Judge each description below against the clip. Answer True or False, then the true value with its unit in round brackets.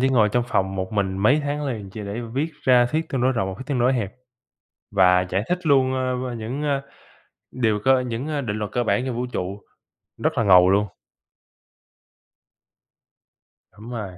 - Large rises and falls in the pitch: False (4.6 semitones)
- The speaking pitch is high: False (120 Hz)